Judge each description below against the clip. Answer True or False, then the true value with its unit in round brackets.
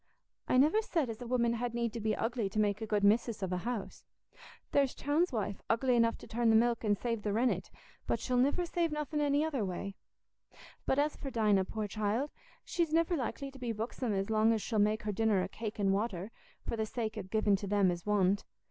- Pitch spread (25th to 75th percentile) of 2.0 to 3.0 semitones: False (3.6 semitones)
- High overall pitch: True (225 Hz)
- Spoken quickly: True (230 wpm)